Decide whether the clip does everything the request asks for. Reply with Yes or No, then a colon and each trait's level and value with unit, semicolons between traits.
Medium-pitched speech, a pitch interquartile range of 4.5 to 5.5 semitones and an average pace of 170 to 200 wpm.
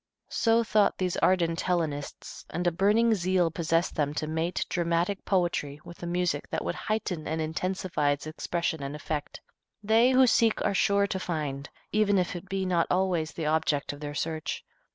No: medium, 175 Hz; average, 3.5 semitones; average, 180 wpm